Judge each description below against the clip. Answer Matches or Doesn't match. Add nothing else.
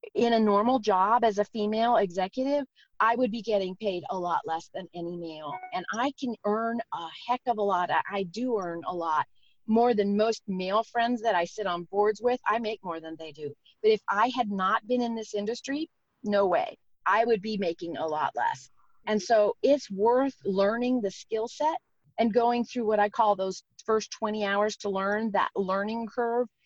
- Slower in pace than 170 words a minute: Doesn't match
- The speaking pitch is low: Doesn't match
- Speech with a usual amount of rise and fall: Matches